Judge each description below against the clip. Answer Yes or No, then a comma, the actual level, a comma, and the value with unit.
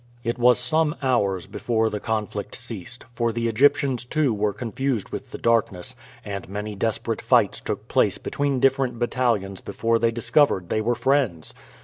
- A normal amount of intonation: Yes, average, 3.3 semitones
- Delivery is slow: No, average, 160 wpm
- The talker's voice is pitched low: Yes, low, 115 Hz